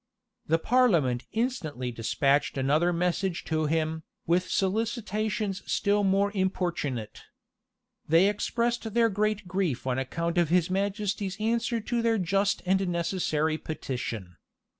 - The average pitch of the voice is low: No, medium, 185 Hz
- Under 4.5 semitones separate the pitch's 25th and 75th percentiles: No, average, 5.0 semitones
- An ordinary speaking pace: No, slow, 125 wpm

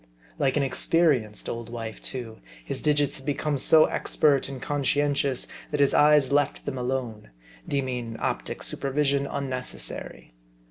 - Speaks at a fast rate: No, slow, 135 wpm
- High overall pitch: No, low, 135 Hz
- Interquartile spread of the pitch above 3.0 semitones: No, narrow, 2.4 semitones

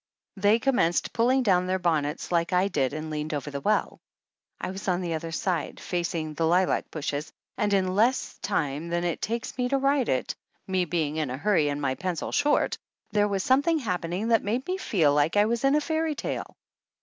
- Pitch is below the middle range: No, medium, 185 Hz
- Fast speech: Yes, fast, 210 wpm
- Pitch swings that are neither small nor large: No, wide, 6.1 semitones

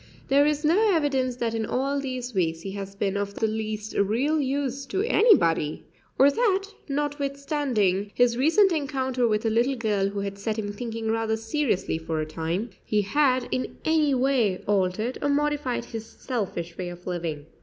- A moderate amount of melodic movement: No, wide, 5.8 semitones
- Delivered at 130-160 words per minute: No, average, 175 wpm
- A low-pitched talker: No, high, 235 Hz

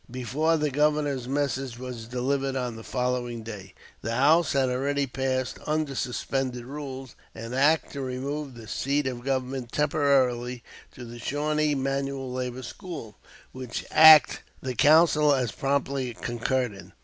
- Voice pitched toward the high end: No, low, 130 Hz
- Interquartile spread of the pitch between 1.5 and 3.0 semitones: Yes, narrow, 2.5 semitones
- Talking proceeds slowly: No, average, 145 wpm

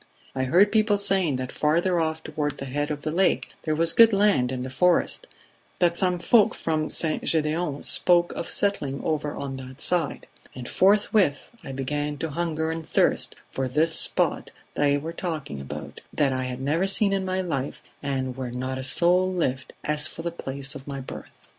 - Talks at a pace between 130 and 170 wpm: No, average, 190 wpm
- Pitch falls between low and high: Yes, medium, 155 Hz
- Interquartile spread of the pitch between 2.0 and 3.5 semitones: No, average, 4.6 semitones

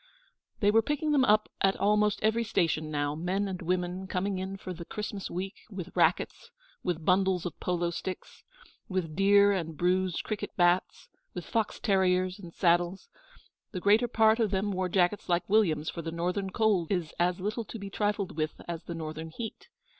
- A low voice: No, medium, 185 Hz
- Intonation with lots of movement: No, average, 2.9 semitones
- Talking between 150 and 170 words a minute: No, average, 185 wpm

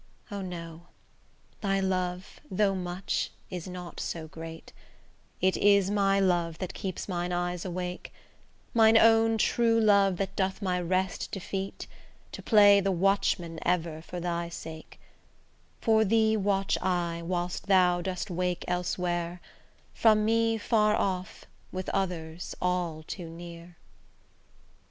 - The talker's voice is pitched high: No, medium, 180 Hz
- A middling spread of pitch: No, narrow, 2.3 semitones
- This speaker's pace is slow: Yes, slow, 130 wpm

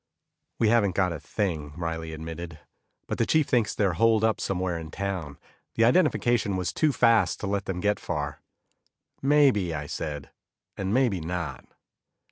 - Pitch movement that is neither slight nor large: No, wide, 5.7 semitones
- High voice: No, very low, 95 Hz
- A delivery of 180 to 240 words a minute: No, average, 160 wpm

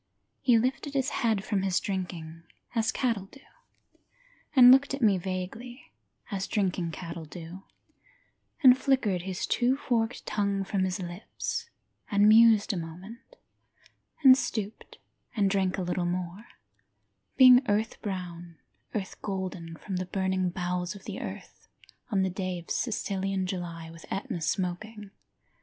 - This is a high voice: Yes, high, 195 Hz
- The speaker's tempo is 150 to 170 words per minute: No, average, 140 wpm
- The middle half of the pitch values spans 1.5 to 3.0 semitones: No, average, 3.8 semitones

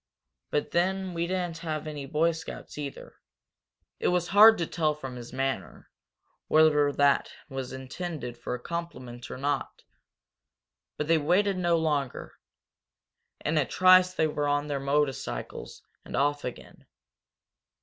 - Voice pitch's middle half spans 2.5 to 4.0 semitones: Yes, average, 3.7 semitones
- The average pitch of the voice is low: No, medium, 150 Hz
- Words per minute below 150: Yes, average, 140 wpm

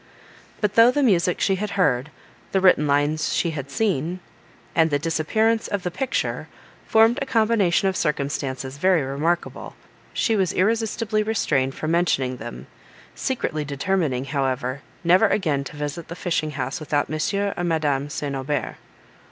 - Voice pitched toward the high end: No, medium, 165 Hz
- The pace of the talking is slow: No, average, 150 wpm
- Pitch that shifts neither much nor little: No, wide, 5.8 semitones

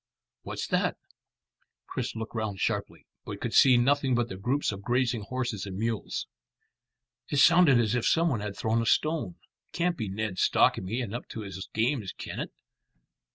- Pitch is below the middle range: Yes, low, 115 Hz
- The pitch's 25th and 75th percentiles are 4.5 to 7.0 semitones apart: No, average, 4.0 semitones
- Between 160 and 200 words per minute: Yes, average, 180 wpm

